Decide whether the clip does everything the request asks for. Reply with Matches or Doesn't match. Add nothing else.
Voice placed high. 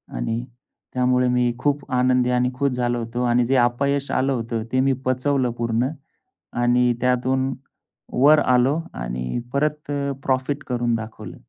Doesn't match